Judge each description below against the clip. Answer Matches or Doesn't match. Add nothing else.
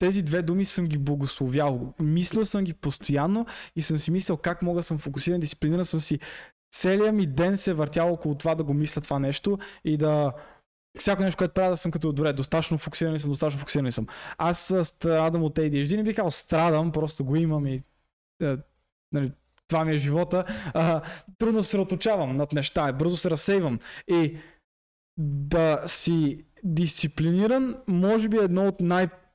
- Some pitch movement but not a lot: Matches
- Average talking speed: Doesn't match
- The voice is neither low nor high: Matches